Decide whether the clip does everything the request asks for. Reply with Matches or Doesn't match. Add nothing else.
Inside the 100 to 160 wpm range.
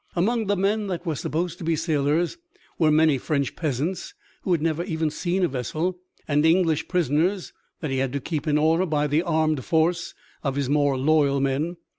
Doesn't match